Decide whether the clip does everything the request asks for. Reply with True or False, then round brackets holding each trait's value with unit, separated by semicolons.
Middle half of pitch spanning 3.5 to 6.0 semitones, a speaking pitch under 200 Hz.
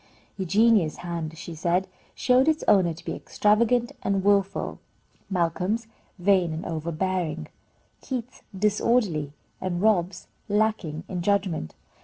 True (3.8 semitones; 190 Hz)